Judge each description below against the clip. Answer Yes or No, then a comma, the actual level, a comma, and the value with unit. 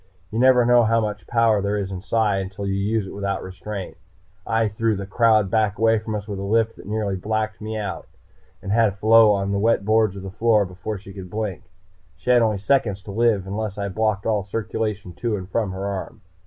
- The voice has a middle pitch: No, low, 105 Hz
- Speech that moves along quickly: Yes, fast, 225 wpm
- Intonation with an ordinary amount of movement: No, narrow, 2.3 semitones